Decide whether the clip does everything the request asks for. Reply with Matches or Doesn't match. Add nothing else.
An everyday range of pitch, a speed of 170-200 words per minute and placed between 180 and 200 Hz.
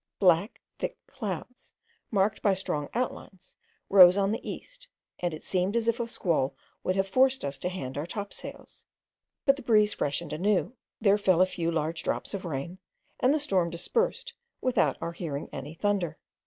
Matches